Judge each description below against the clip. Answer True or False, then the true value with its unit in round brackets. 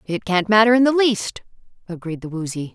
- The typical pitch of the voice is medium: False (200 Hz)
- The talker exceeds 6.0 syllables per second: False (5.4 syllables/s)